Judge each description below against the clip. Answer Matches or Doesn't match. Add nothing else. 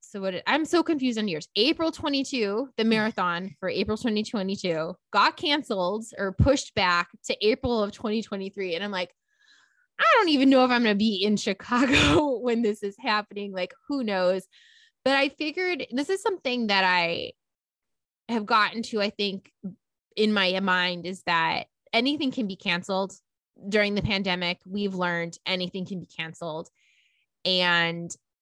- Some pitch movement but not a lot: Doesn't match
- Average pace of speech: Matches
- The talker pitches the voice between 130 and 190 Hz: Doesn't match